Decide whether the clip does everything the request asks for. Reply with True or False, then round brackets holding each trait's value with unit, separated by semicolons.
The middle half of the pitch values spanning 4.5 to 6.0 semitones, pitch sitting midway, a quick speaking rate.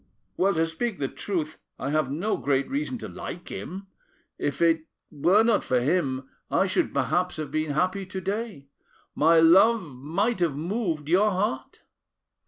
False (5.0 semitones; 170 Hz; 165 wpm)